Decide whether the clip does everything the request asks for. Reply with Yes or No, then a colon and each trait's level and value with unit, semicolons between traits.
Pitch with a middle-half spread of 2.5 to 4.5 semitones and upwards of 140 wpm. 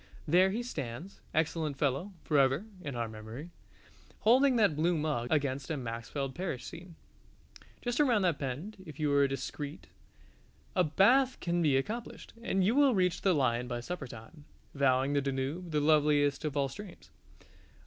No: average, 5.2 semitones; average, 160 wpm